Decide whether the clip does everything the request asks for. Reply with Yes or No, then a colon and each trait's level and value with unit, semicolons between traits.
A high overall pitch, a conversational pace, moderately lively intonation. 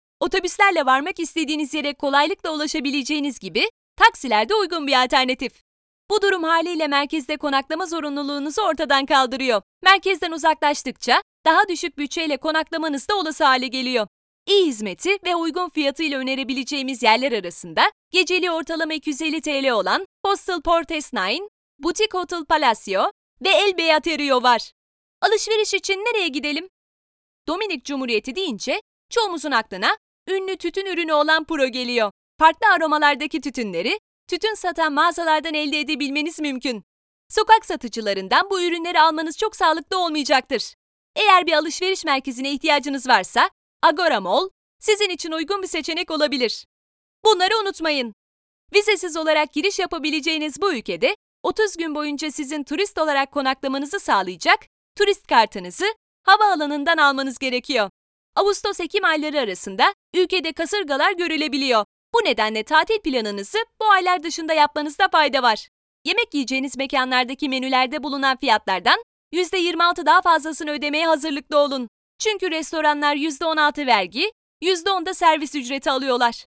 Yes: very high, 315 Hz; average, 125 wpm; average, 4.8 semitones